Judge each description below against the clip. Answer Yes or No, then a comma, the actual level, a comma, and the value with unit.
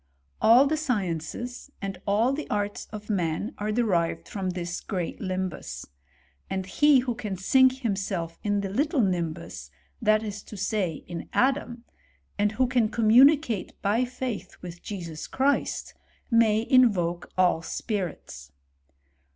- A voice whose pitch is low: No, high, 205 Hz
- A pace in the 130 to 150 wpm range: Yes, average, 145 wpm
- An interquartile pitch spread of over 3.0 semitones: Yes, average, 5.0 semitones